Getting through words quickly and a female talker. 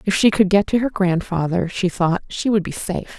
Yes: fast, 245 wpm; female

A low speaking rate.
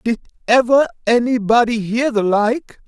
Yes: slow, 125 wpm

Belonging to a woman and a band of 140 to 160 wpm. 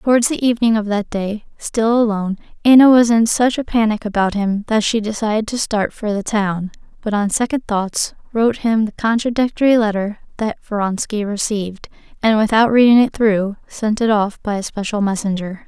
No: female; average, 185 wpm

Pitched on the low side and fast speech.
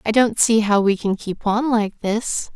No: high, 215 Hz; fast, 235 wpm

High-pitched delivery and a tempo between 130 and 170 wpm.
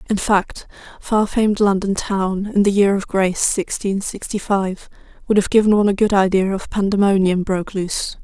No: high, 200 Hz; average, 180 wpm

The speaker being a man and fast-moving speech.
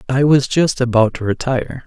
No: male; average, 195 wpm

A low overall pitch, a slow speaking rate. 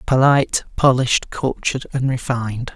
Yes: low, 130 Hz; slow, 110 wpm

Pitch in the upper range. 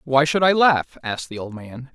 No: medium, 140 Hz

